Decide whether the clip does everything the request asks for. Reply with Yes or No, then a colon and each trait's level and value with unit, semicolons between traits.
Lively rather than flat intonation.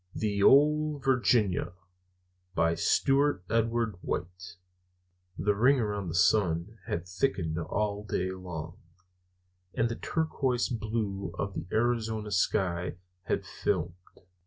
No: average, 4.7 semitones